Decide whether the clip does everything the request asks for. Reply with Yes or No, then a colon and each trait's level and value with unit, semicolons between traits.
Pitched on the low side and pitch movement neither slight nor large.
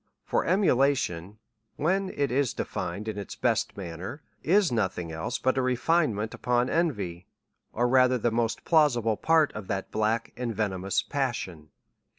No: low, 120 Hz; wide, 5.8 semitones